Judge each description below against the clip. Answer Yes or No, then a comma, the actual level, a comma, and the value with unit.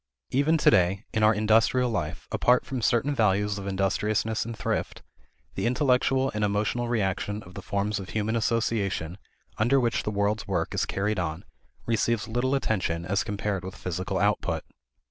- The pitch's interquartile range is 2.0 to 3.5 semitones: Yes, average, 3.1 semitones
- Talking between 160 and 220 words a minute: Yes, average, 165 wpm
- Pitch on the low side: Yes, low, 105 Hz